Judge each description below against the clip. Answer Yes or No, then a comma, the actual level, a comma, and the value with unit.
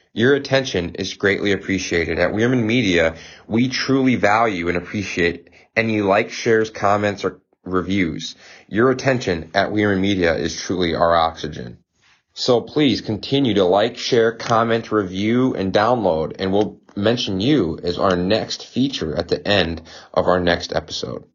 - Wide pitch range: No, average, 4.1 semitones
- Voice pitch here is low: Yes, low, 100 Hz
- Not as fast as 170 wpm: Yes, average, 150 wpm